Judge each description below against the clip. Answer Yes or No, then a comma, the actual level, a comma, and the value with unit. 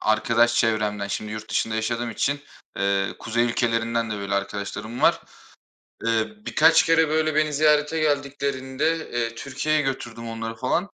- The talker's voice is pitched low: Yes, low, 120 Hz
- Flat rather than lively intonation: No, average, 4.6 semitones